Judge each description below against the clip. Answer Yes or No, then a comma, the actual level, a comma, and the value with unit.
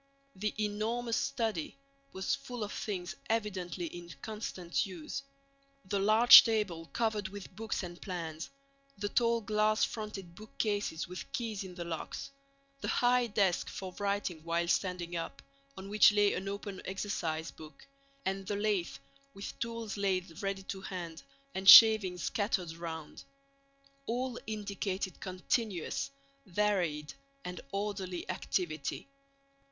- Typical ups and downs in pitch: Yes, average, 3.3 semitones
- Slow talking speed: Yes, slow, 125 wpm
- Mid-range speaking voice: No, high, 195 Hz